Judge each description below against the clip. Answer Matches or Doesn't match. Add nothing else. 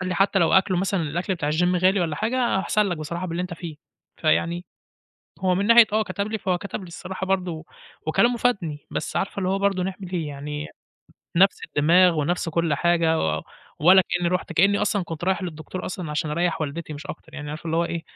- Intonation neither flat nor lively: Matches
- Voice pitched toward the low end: Doesn't match